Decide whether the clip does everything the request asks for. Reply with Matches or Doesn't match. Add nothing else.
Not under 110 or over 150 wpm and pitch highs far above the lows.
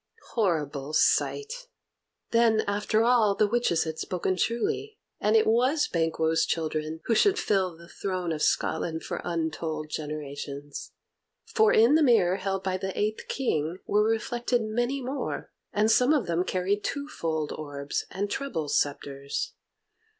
Matches